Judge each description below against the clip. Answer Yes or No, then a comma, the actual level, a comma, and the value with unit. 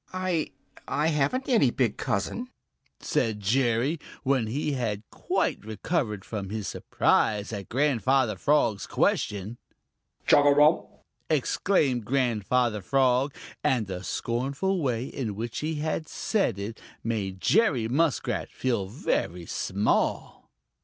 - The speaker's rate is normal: No, slow, 110 wpm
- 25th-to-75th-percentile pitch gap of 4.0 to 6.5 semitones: Yes, average, 5.3 semitones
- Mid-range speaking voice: No, low, 125 Hz